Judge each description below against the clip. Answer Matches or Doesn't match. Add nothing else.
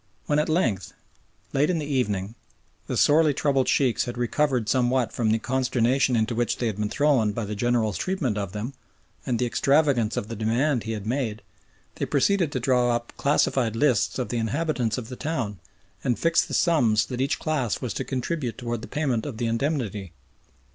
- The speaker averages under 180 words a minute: Doesn't match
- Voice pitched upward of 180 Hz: Doesn't match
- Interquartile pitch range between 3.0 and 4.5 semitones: Matches